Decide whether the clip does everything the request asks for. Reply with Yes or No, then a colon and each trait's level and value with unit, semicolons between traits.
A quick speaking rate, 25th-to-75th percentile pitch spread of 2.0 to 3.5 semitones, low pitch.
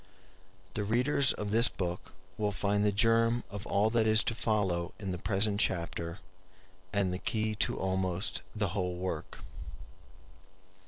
No: average, 150 wpm; average, 3.0 semitones; low, 100 Hz